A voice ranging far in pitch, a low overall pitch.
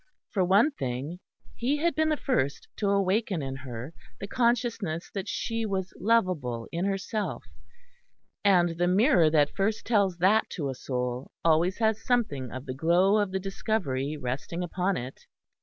No: wide, 6.8 semitones; medium, 185 Hz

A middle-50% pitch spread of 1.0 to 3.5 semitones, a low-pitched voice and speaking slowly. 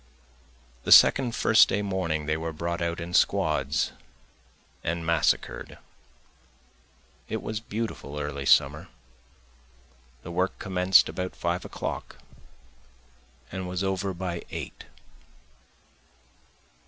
Yes: narrow, 2.4 semitones; very low, 90 Hz; slow, 105 wpm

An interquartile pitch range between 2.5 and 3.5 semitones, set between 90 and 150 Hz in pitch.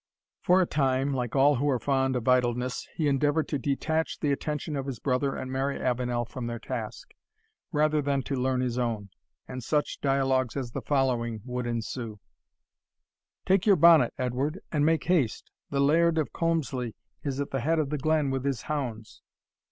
Yes: average, 3.1 semitones; low, 135 Hz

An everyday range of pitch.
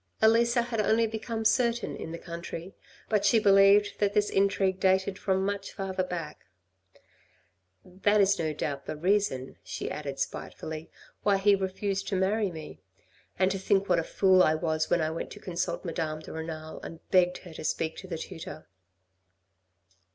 Yes: average, 3.7 semitones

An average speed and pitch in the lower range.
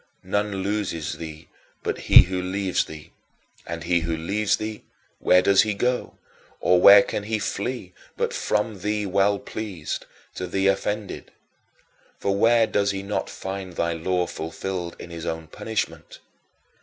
Yes: average, 155 wpm; very low, 95 Hz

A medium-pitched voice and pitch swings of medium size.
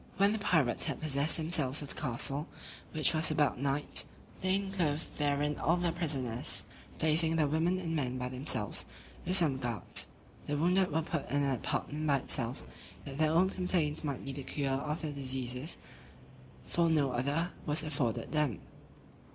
Yes: medium, 150 Hz; average, 3.1 semitones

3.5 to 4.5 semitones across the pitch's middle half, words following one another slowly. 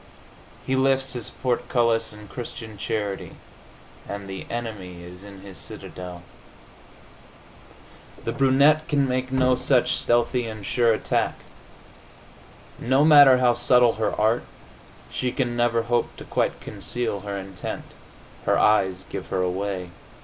Yes: average, 4.1 semitones; slow, 130 wpm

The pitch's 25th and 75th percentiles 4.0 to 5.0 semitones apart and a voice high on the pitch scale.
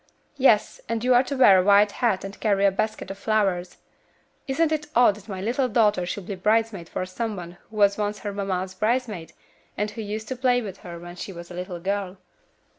No: average, 3.3 semitones; high, 205 Hz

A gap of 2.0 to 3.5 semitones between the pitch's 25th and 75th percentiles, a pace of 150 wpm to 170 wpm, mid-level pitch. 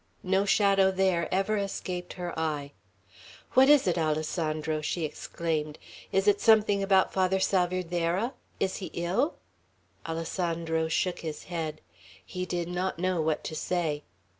No: average, 2.9 semitones; average, 140 wpm; medium, 180 Hz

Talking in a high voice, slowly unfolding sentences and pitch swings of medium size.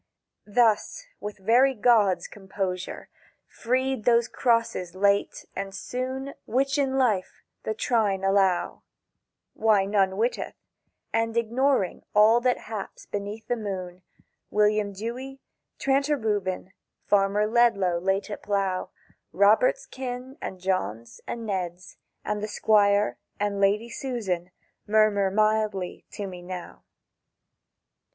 Yes: high, 210 Hz; slow, 115 wpm; average, 3.6 semitones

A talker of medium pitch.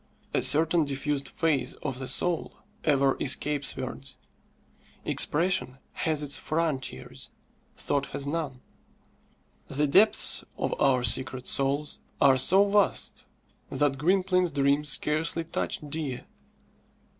Yes: medium, 145 Hz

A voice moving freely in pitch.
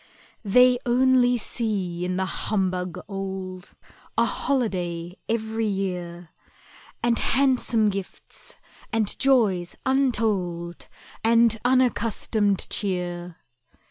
No: average, 4.7 semitones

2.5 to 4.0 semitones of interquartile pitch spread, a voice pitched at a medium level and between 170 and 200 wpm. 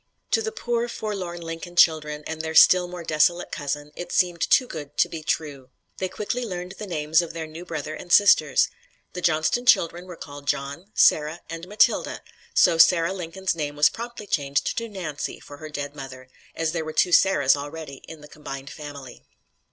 Yes: average, 3.3 semitones; medium, 165 Hz; average, 190 wpm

